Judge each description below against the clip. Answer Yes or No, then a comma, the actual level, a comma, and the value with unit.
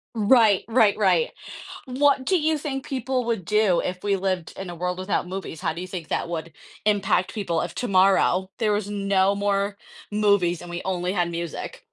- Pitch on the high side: Yes, high, 195 Hz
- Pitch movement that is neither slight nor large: Yes, average, 3.2 semitones